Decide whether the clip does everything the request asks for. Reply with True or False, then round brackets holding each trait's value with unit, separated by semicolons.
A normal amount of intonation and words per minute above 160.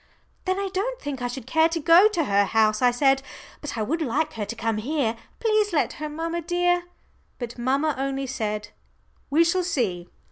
False (6.3 semitones; 200 wpm)